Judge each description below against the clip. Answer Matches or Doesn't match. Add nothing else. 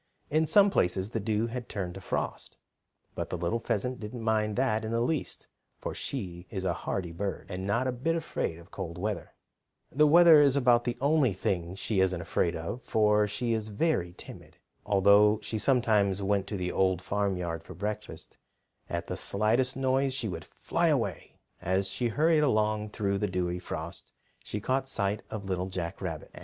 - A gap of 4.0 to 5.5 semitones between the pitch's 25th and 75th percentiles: Matches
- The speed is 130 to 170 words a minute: Doesn't match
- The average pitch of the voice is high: Doesn't match